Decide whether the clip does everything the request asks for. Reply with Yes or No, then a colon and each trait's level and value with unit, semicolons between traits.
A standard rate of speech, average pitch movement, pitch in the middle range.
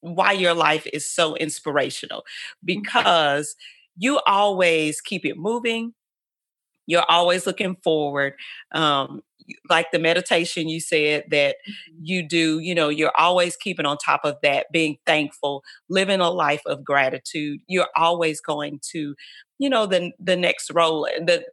Yes: average, 145 wpm; average, 3.3 semitones; medium, 170 Hz